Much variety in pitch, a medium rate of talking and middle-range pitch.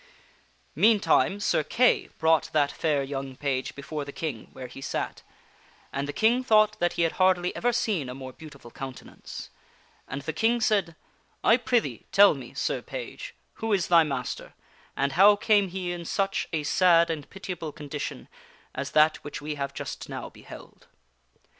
Yes: wide, 5.9 semitones; average, 170 wpm; medium, 160 Hz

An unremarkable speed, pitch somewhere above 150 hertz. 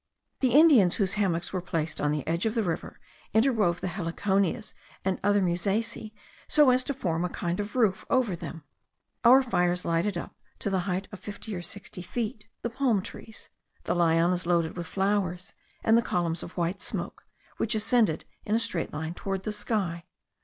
Yes: average, 185 wpm; high, 190 Hz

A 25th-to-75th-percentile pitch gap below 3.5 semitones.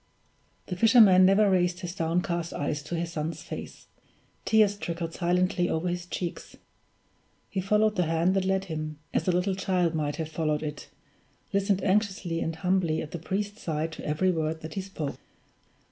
Yes: average, 3.0 semitones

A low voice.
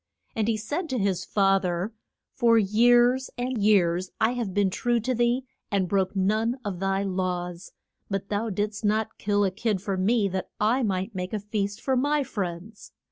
No: high, 205 Hz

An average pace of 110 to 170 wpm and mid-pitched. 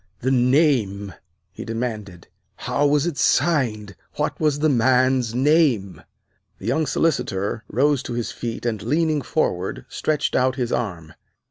No: average, 140 wpm; low, 125 Hz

